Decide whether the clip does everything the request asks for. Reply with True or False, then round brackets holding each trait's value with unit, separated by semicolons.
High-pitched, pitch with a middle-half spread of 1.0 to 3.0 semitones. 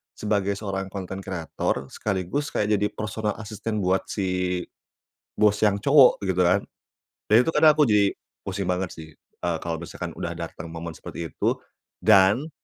False (100 Hz; 2.6 semitones)